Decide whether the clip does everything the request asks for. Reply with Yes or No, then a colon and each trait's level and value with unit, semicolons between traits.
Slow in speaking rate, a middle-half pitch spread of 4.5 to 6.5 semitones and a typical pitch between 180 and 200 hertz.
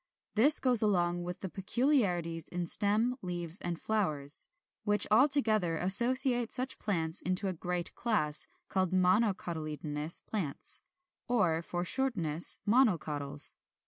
Yes: slow, 115 wpm; average, 5.1 semitones; medium, 185 Hz